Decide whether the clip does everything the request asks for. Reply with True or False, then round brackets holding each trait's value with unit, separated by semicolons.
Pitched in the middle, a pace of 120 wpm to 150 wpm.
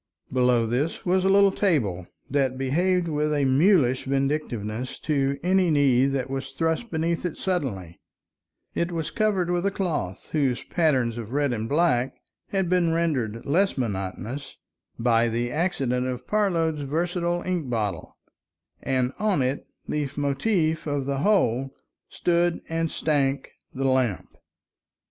True (145 Hz; 140 wpm)